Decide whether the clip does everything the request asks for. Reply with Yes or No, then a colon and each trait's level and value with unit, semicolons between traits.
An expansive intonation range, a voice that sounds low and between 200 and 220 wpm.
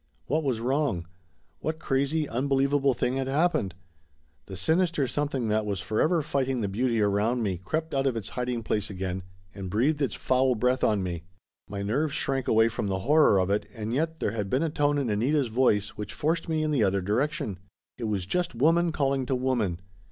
Yes: wide, 5.7 semitones; low, 125 Hz; fast, 205 wpm